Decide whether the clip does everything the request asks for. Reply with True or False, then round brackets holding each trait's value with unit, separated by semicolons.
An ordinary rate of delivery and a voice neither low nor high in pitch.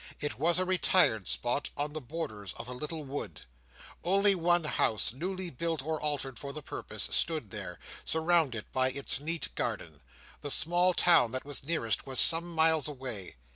True (175 wpm; 150 Hz)